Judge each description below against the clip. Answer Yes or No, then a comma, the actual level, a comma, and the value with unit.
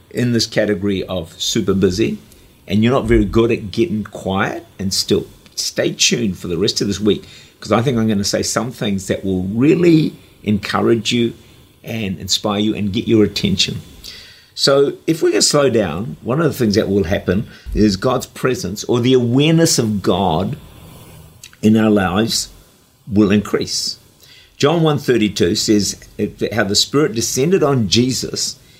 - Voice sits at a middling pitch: No, low, 110 Hz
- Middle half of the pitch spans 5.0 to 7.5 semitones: No, average, 3.2 semitones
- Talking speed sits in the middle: Yes, average, 170 wpm